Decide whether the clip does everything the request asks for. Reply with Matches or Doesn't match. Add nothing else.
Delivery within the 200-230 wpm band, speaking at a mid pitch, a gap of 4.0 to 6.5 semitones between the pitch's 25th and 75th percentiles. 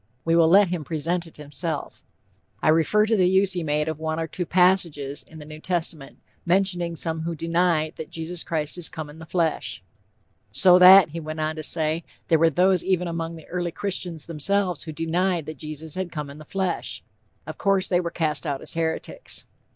Doesn't match